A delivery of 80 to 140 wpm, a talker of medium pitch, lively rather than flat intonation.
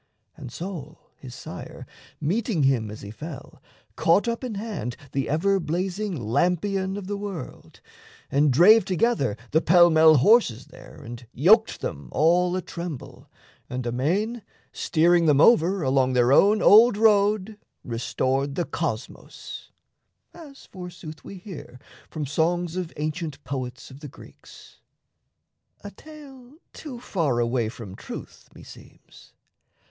Yes: slow, 135 wpm; medium, 165 Hz; wide, 6.9 semitones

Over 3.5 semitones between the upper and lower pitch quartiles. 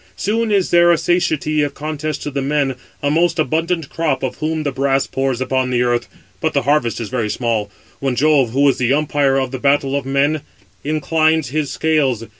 No: average, 2.9 semitones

